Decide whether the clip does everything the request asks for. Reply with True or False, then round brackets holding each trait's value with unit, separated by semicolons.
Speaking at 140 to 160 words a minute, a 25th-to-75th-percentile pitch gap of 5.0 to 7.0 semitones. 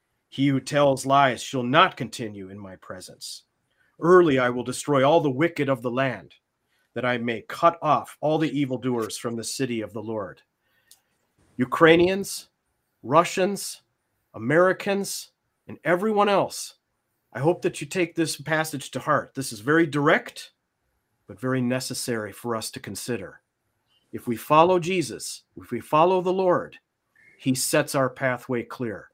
True (150 wpm; 5.5 semitones)